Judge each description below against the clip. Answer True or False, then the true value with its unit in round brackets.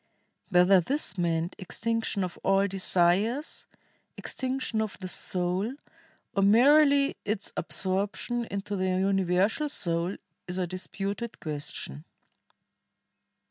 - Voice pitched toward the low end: False (195 Hz)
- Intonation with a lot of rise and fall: False (4.0 semitones)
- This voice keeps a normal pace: False (100 wpm)